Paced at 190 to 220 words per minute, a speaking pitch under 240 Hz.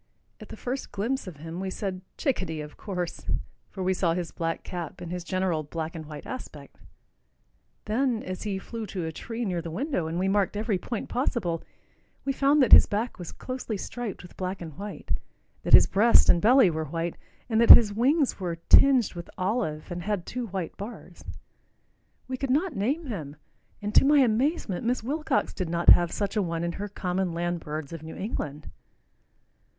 Yes: average, 195 wpm; high, 190 Hz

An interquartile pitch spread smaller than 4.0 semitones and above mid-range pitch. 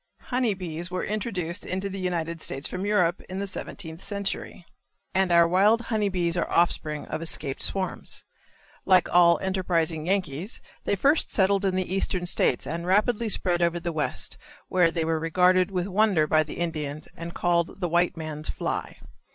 No: average, 2.7 semitones; medium, 180 Hz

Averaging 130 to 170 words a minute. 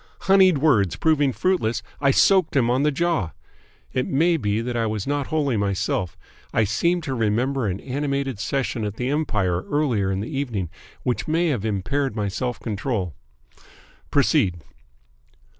Yes: average, 160 wpm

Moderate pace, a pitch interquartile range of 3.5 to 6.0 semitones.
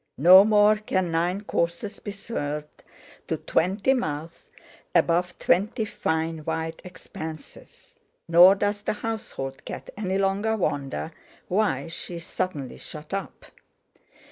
No: slow, 120 wpm; average, 4.1 semitones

